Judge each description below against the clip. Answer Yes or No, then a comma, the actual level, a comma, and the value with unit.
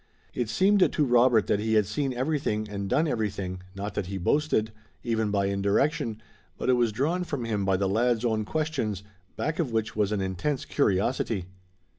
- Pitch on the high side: No, low, 110 Hz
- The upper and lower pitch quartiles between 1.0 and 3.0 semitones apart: No, average, 4.7 semitones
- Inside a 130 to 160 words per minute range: No, average, 185 wpm